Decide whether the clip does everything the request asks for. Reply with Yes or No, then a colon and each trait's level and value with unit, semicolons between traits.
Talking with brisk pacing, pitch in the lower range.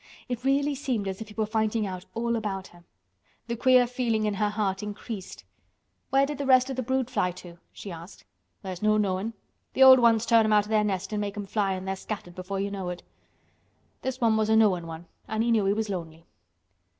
No: fast, 230 wpm; high, 215 Hz